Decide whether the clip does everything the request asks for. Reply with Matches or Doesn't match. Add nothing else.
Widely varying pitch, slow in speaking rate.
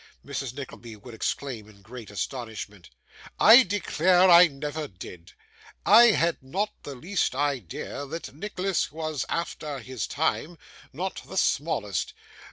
Matches